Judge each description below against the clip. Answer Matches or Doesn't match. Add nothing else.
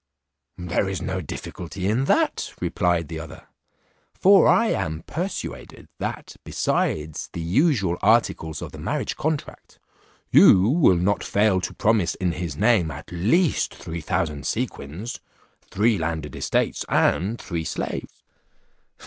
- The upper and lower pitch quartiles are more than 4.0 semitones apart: Matches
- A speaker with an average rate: Doesn't match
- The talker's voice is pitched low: Matches